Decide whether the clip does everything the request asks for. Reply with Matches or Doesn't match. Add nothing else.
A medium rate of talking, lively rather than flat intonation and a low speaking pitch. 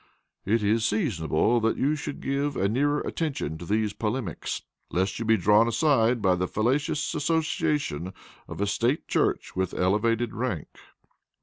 Matches